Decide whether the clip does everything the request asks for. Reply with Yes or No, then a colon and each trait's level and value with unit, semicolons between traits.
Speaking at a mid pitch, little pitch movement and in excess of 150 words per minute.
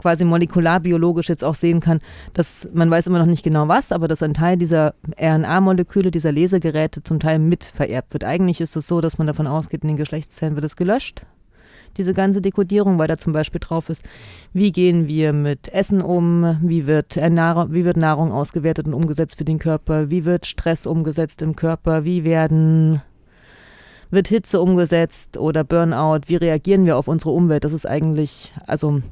Yes: medium, 165 Hz; narrow, 1.8 semitones; average, 185 wpm